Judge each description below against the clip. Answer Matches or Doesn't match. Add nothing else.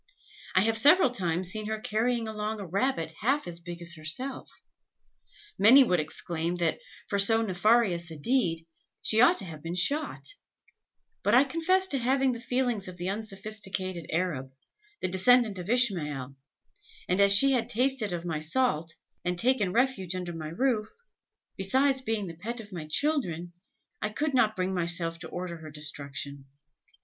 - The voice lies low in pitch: Doesn't match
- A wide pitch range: Matches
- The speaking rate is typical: Matches